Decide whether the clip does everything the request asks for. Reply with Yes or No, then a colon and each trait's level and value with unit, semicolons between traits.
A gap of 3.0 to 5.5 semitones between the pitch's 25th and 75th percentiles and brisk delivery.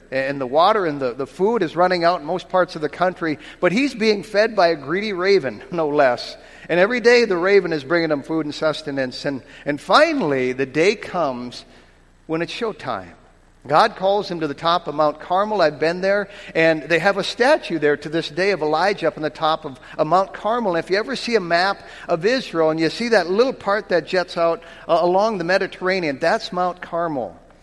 Yes: average, 4.0 semitones; fast, 220 wpm